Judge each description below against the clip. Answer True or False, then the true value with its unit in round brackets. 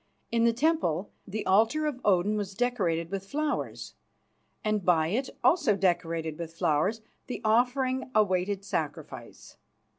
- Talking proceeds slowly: True (130 wpm)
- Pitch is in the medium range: False (205 Hz)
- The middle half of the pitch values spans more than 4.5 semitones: True (5.6 semitones)